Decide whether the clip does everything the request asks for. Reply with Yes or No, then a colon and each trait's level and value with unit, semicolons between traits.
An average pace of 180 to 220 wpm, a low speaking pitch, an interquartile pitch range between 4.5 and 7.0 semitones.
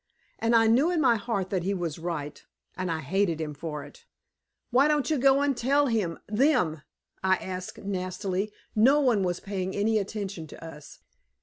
No: average, 185 wpm; high, 200 Hz; wide, 5.6 semitones